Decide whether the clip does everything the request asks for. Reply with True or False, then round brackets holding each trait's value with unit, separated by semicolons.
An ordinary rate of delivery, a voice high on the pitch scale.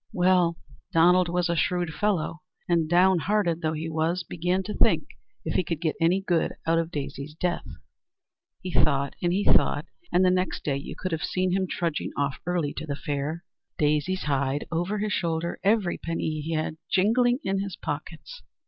False (185 wpm; 170 Hz)